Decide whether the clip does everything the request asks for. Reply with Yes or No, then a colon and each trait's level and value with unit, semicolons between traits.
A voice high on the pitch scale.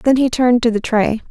Yes: high, 240 Hz